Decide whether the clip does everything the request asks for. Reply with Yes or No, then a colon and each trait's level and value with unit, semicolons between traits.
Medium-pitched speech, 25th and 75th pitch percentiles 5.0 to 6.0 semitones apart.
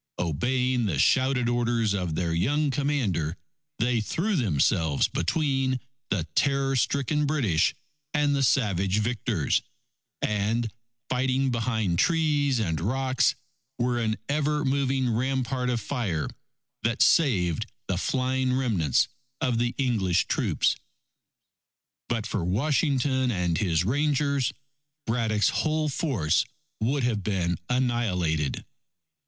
No: low, 120 Hz; wide, 5.5 semitones